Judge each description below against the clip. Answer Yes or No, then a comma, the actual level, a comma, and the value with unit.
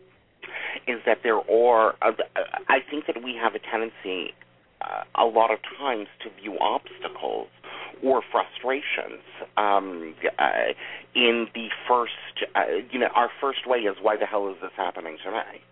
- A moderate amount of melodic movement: Yes, average, 4.1 semitones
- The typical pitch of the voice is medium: No, low, 115 Hz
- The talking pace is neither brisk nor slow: Yes, average, 155 wpm